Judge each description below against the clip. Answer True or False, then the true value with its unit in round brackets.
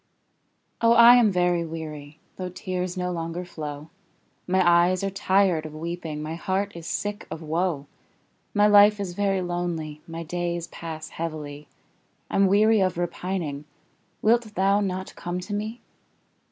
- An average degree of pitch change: True (3.2 semitones)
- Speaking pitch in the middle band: True (175 Hz)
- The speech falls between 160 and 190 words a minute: False (150 wpm)